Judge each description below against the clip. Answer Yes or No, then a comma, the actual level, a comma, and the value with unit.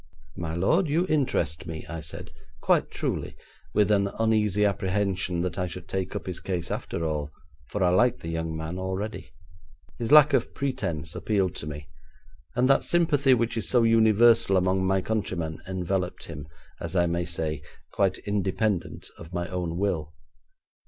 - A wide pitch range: No, average, 4.6 semitones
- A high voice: No, very low, 95 Hz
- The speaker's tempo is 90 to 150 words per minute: No, average, 165 wpm